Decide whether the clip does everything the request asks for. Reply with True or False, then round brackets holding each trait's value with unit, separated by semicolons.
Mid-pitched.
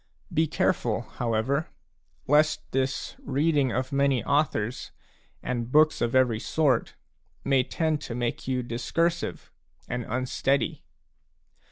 False (130 Hz)